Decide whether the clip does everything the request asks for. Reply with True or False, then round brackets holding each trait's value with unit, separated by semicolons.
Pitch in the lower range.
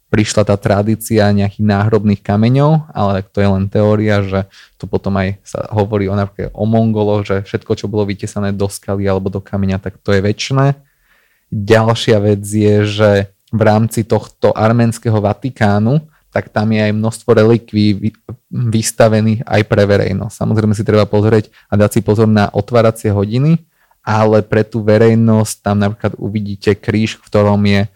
True (105 Hz)